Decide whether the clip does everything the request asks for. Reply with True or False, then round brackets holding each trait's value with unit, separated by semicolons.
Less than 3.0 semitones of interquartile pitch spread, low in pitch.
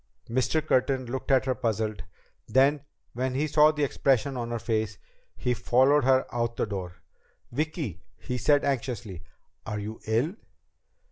False (3.8 semitones; 125 Hz)